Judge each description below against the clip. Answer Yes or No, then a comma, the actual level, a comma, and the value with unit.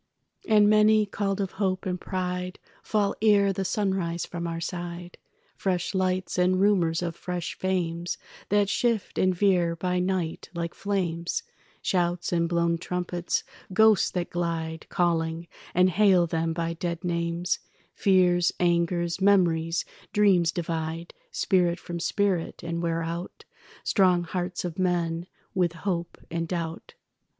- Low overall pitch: No, medium, 175 Hz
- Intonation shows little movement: Yes, narrow, 1.9 semitones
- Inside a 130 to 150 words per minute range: Yes, slow, 135 wpm